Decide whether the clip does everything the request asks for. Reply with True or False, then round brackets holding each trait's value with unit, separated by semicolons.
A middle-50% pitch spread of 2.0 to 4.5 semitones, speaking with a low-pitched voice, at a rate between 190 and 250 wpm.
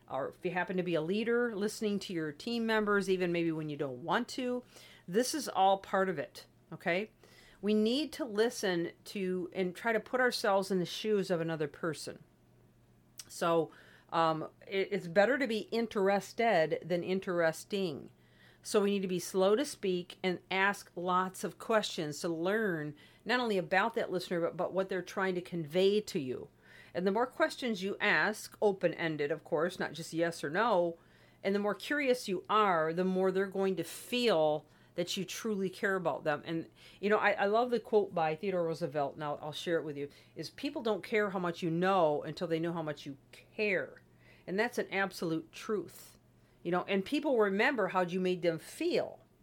False (4.1 semitones; 190 Hz; 195 wpm)